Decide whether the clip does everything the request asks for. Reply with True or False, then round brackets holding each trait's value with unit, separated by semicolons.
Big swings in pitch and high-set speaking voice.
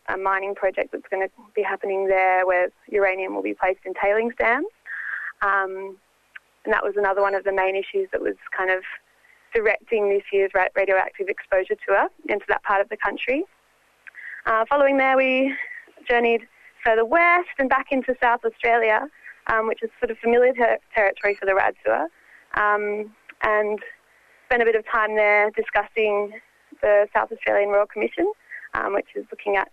False (4.6 semitones; 215 Hz)